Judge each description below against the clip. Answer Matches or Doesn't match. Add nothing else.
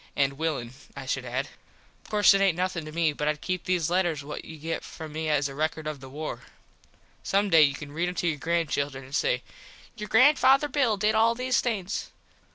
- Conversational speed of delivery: Doesn't match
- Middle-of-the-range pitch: Matches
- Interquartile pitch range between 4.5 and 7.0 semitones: Matches